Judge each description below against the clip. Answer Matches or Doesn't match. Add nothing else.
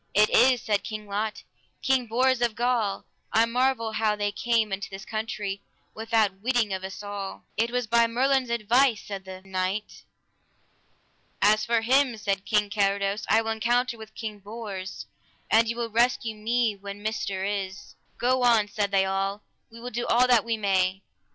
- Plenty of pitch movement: Doesn't match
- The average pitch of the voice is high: Matches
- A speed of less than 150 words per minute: Doesn't match